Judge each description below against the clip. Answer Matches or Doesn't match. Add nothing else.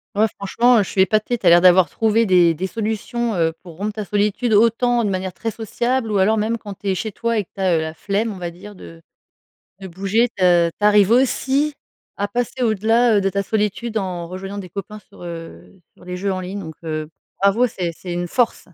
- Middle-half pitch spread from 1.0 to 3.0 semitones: Doesn't match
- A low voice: Doesn't match